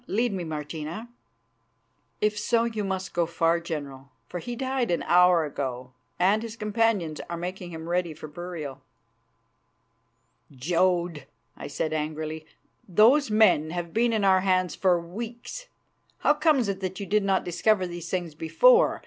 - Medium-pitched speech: Yes, medium, 180 Hz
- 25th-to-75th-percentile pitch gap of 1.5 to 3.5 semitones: No, average, 4.7 semitones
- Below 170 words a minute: Yes, average, 155 wpm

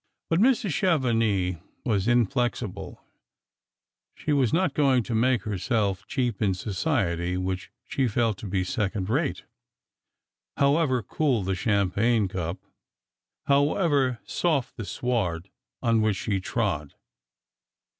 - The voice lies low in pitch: Yes, low, 115 Hz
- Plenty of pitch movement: Yes, wide, 5.7 semitones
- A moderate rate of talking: No, slow, 120 wpm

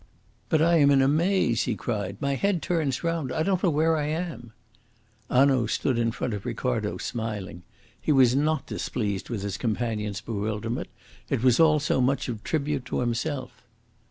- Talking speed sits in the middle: Yes, average, 180 wpm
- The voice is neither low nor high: No, low, 130 Hz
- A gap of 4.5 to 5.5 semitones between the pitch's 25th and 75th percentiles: Yes, average, 5.2 semitones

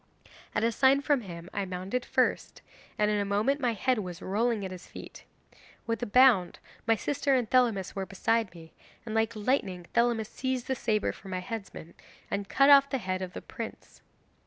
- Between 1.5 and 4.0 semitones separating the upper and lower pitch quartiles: No, average, 4.8 semitones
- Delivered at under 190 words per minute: No, average, 195 wpm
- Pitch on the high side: Yes, high, 220 Hz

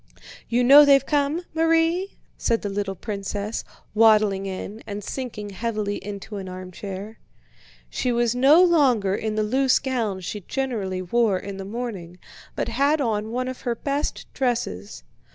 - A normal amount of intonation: Yes, average, 4.8 semitones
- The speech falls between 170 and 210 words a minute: No, average, 150 wpm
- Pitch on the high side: Yes, high, 220 Hz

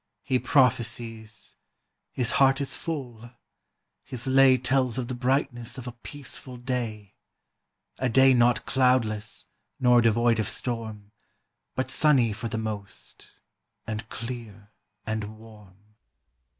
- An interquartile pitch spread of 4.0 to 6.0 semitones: No, average, 2.8 semitones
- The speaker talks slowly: Yes, slow, 120 wpm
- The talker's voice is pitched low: Yes, low, 120 Hz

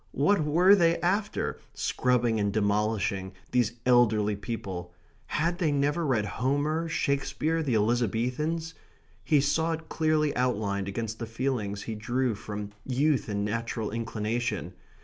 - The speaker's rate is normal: No, slow, 130 wpm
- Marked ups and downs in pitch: Yes, wide, 6.1 semitones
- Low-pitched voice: Yes, low, 120 Hz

